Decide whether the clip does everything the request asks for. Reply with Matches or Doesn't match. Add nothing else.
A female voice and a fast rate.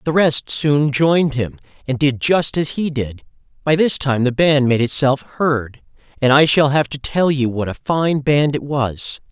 Doesn't match